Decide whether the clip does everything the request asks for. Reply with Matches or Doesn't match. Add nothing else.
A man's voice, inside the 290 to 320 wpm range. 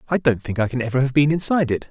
Matches